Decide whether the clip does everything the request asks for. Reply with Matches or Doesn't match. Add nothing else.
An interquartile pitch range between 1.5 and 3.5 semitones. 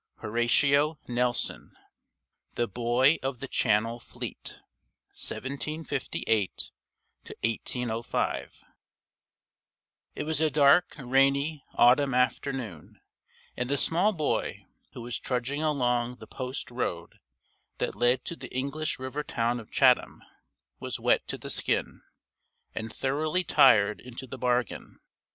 Matches